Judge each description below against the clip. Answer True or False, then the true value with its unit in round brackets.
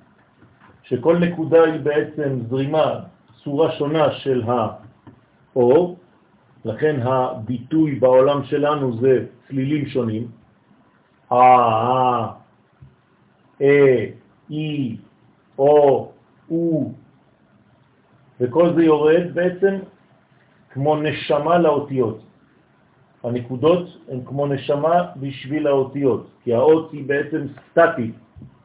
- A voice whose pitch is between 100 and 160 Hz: True (140 Hz)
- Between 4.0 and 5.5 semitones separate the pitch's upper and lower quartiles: False (3.4 semitones)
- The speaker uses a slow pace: True (80 wpm)